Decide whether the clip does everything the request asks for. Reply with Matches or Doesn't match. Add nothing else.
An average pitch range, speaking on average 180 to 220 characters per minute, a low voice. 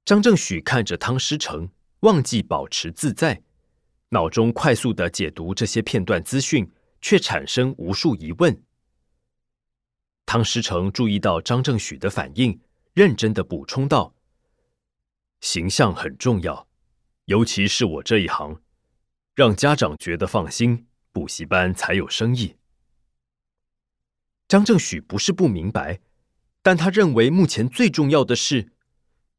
Doesn't match